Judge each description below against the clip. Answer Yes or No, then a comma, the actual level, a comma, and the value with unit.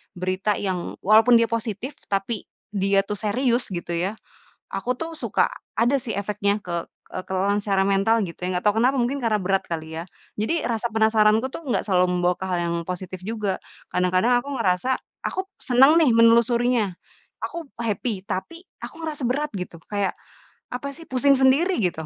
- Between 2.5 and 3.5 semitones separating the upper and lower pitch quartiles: No, average, 4.7 semitones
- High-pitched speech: Yes, high, 215 Hz